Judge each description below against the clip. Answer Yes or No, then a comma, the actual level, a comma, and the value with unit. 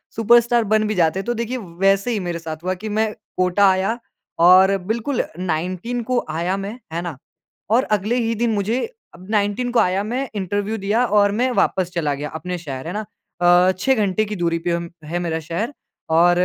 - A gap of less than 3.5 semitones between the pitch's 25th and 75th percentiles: No, average, 4.3 semitones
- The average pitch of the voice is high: Yes, high, 195 Hz